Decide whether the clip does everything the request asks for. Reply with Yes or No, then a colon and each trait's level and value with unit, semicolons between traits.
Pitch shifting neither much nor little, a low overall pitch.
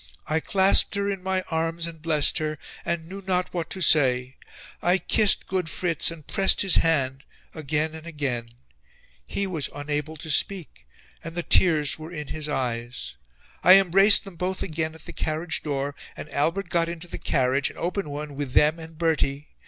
No: average, 3.4 semitones; medium, 160 Hz